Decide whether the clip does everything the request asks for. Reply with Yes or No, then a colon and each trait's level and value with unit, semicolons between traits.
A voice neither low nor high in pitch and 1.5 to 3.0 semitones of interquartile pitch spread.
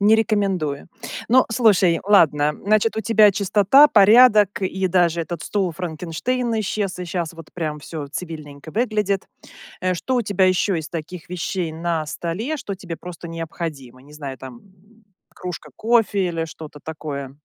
No: medium, 180 Hz; average, 4.6 semitones